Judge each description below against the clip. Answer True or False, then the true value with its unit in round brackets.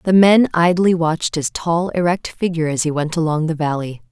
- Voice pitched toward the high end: False (165 Hz)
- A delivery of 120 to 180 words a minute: False (205 wpm)